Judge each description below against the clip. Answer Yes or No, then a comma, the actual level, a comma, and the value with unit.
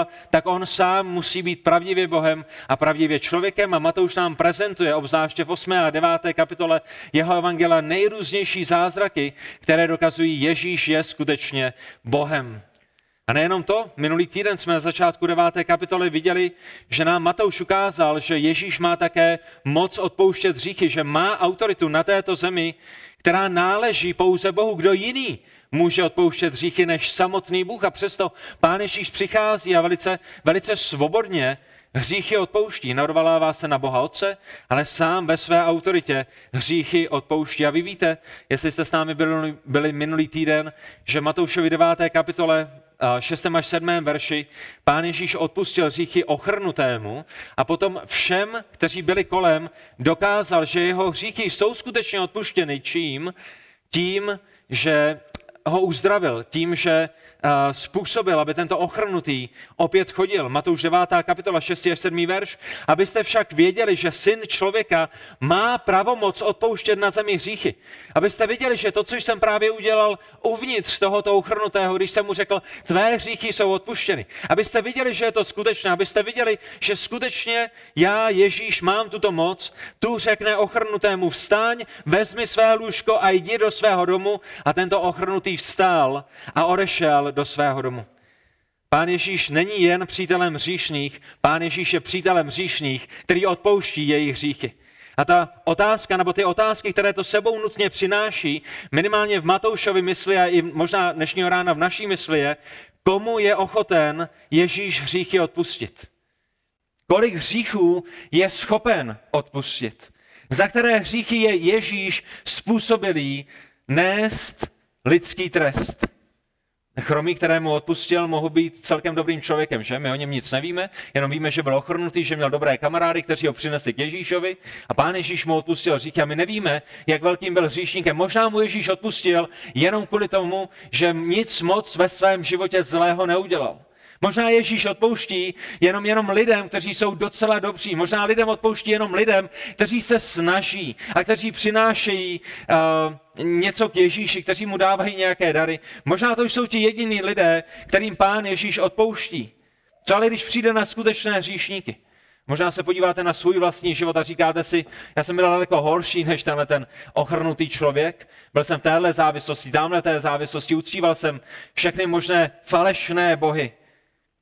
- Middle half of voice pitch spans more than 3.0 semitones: Yes, average, 4.2 semitones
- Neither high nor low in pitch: Yes, medium, 180 Hz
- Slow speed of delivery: No, average, 150 wpm